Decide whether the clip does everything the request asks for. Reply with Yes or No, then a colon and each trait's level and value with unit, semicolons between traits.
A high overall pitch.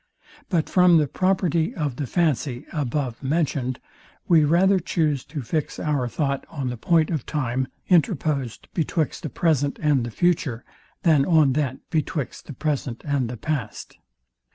No: medium, 150 Hz